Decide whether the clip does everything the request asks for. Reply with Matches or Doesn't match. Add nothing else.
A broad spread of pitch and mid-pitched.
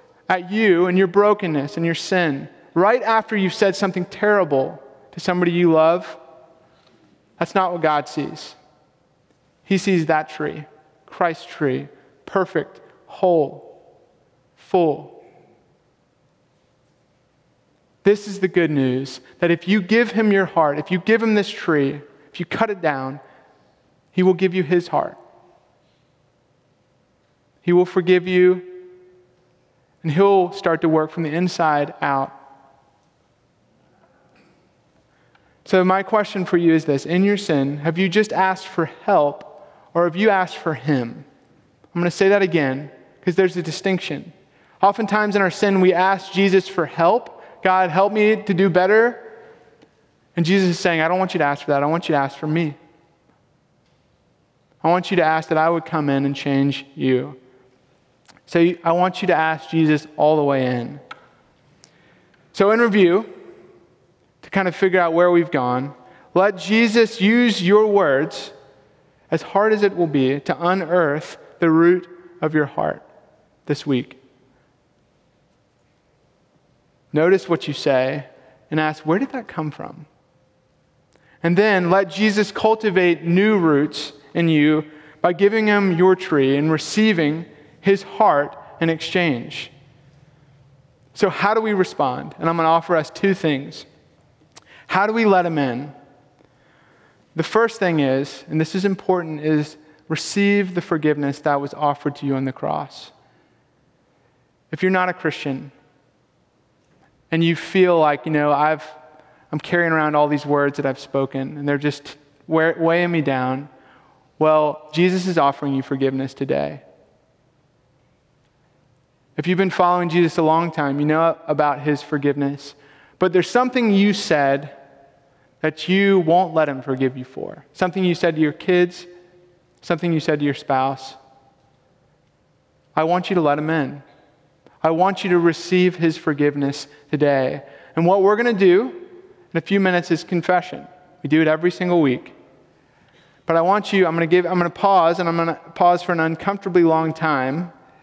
Doesn't match